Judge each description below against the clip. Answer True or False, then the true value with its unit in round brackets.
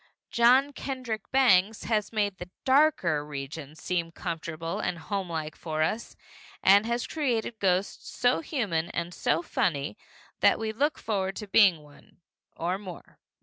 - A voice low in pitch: False (195 Hz)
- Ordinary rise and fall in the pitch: False (5.8 semitones)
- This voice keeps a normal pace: True (145 wpm)